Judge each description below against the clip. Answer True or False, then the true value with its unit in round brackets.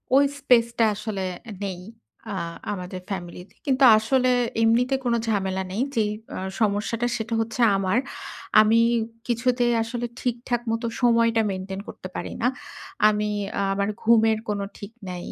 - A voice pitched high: True (225 Hz)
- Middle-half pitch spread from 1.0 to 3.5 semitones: True (3.2 semitones)